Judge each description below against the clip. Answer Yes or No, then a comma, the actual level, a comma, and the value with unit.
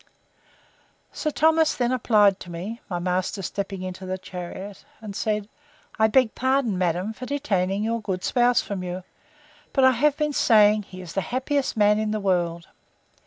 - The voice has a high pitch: Yes, high, 210 Hz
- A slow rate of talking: No, average, 170 wpm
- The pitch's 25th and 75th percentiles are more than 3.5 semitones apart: Yes, average, 4.8 semitones